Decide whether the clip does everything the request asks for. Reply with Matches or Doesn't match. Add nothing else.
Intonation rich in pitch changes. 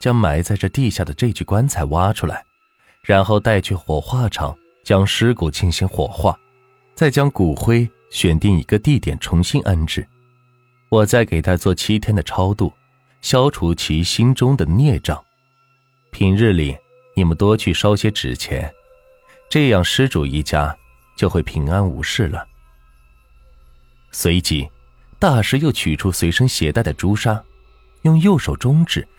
Matches